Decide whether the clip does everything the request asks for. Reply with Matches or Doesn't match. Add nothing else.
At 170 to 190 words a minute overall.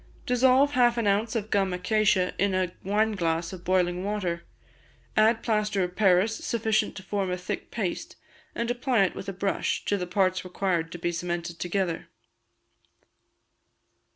Doesn't match